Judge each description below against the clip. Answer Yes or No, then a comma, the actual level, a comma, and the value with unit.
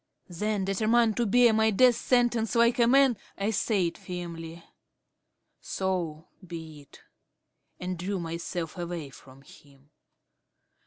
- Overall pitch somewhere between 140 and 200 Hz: Yes, medium, 185 Hz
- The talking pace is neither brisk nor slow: No, slow, 120 wpm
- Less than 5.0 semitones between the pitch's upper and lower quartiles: No, average, 5.3 semitones